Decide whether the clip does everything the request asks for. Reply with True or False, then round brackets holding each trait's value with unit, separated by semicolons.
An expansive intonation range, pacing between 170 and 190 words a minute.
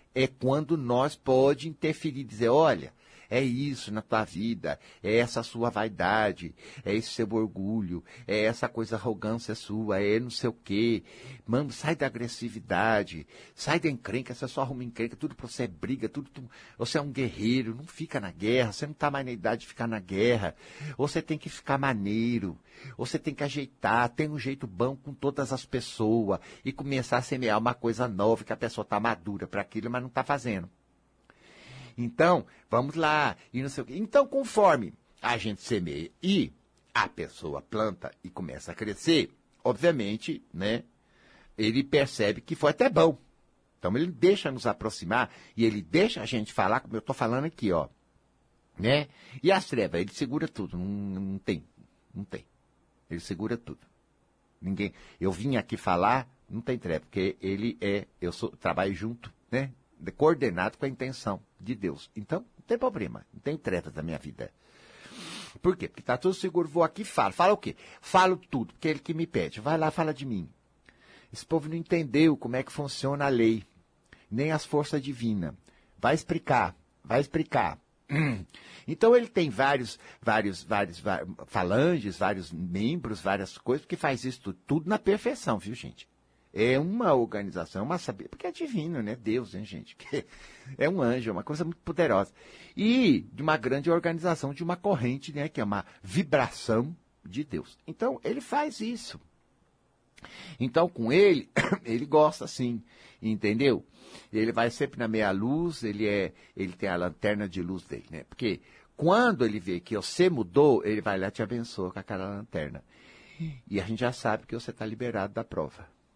True (5.7 semitones; 180 wpm)